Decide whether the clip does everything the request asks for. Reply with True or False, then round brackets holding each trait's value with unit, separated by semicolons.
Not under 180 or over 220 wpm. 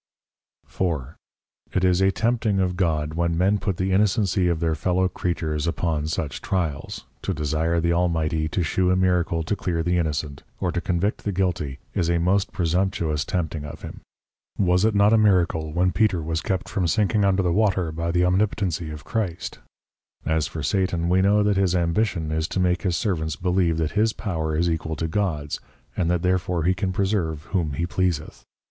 True (190 wpm)